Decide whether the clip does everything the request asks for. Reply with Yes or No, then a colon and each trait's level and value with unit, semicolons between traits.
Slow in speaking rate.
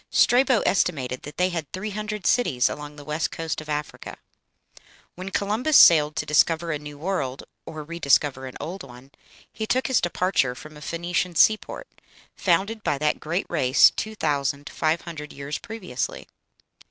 No: average, 165 wpm